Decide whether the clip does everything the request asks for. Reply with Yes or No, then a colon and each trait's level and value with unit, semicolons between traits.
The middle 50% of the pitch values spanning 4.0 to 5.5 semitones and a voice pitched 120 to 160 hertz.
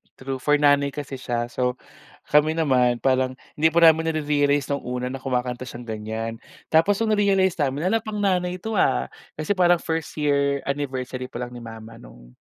Yes: average, 4.5 semitones; medium, 140 Hz